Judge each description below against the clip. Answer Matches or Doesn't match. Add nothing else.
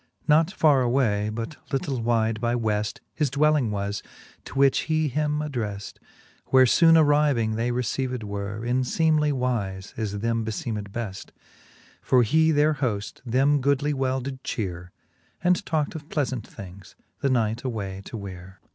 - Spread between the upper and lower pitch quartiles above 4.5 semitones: Matches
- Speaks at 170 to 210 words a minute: Doesn't match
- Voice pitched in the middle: Doesn't match